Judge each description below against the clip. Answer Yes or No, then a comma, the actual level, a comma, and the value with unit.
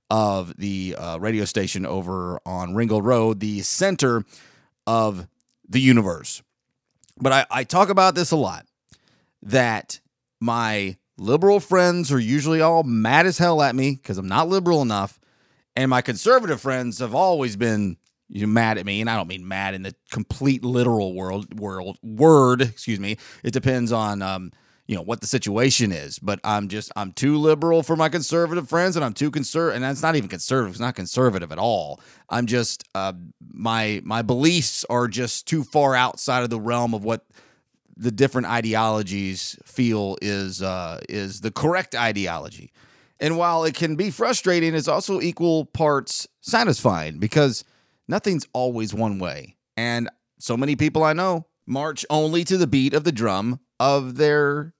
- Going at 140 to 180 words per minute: Yes, average, 170 wpm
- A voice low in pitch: Yes, low, 125 Hz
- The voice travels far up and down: Yes, wide, 6.7 semitones